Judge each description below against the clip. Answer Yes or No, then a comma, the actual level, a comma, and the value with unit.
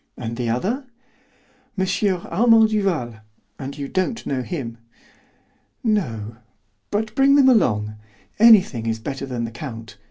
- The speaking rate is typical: No, slow, 130 wpm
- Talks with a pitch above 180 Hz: No, medium, 140 Hz